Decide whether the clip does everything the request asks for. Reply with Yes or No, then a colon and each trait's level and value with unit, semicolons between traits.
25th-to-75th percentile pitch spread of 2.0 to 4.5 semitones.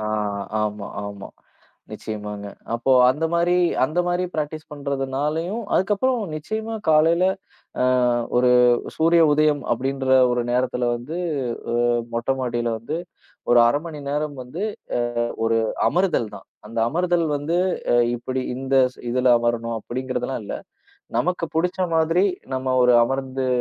No: average, 5.2 semitones